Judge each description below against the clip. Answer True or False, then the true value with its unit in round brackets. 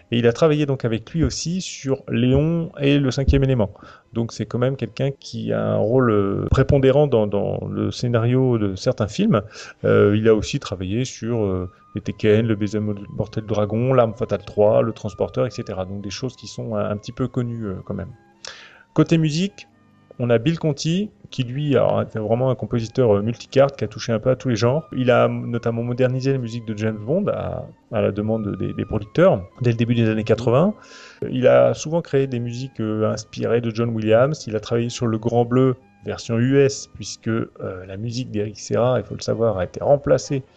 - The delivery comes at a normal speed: True (210 wpm)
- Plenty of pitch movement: False (3.6 semitones)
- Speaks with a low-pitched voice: True (120 Hz)